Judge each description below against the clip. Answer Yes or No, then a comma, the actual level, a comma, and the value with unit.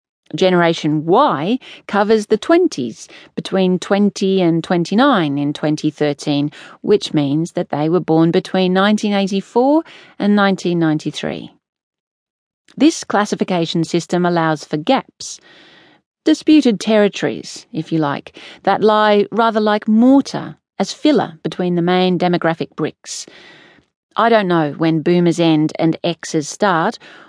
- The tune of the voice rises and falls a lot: No, average, 4.7 semitones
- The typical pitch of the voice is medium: Yes, medium, 180 Hz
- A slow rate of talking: Yes, slow, 115 wpm